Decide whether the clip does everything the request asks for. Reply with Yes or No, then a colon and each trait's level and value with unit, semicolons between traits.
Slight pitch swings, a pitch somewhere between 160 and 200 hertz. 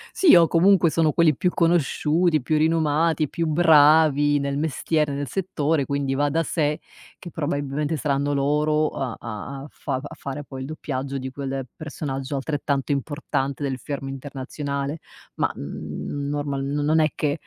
No: narrow, 2.2 semitones; medium, 145 Hz